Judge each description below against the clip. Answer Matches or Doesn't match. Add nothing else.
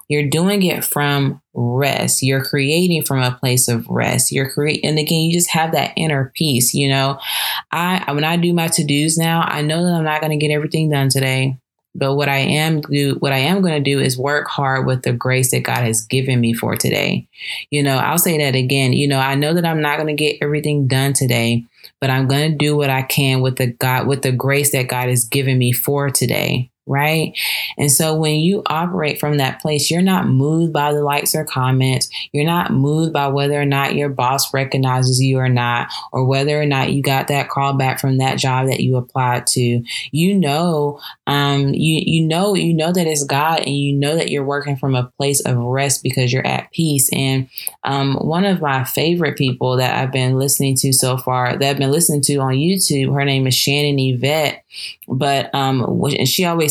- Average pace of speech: Doesn't match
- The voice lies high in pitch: Doesn't match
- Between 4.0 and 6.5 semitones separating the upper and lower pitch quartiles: Doesn't match